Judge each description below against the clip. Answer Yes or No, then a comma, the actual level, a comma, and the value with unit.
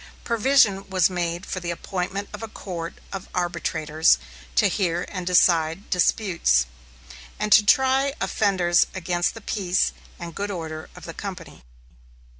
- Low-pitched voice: No, medium, 180 Hz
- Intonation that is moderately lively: Yes, average, 3.1 semitones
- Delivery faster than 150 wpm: No, average, 140 wpm